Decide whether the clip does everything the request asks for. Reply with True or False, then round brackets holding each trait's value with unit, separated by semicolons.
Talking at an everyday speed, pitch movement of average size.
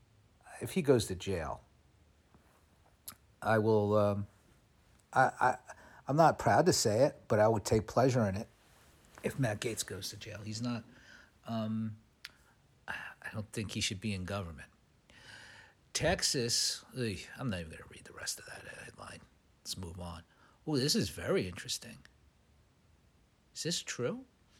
True (155 wpm; 3.3 semitones)